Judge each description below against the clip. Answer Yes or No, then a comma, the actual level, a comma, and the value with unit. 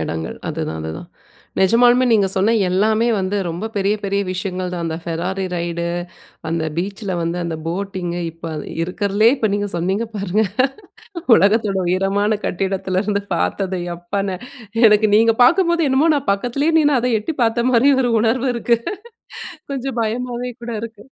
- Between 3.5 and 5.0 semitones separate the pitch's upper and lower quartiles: Yes, average, 4.2 semitones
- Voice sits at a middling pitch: No, high, 200 Hz